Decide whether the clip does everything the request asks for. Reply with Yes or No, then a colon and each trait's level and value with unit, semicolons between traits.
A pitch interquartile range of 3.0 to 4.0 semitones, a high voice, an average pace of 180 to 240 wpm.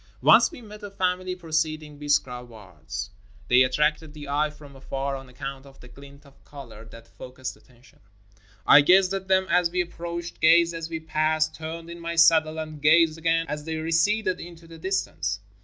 No: average, 3.6 semitones; medium, 155 Hz; average, 190 wpm